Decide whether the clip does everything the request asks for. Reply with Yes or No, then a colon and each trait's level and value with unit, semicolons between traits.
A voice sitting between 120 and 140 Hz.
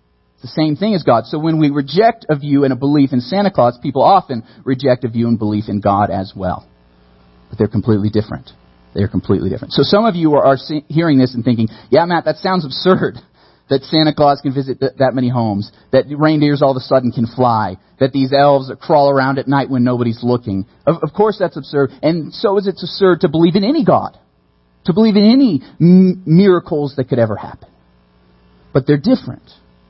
Yes: low, 135 Hz